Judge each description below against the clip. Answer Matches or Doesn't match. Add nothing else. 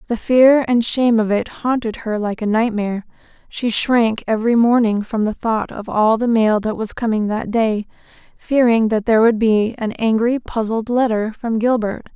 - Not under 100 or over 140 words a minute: Doesn't match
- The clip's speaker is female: Matches